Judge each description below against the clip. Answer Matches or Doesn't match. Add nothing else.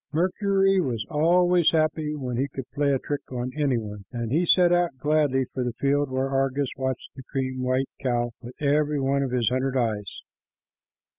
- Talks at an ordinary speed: Matches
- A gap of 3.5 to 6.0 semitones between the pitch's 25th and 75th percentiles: Doesn't match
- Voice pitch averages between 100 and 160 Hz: Matches